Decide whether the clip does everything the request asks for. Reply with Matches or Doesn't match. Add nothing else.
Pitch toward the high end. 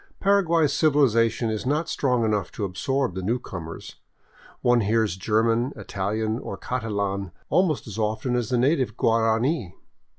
Doesn't match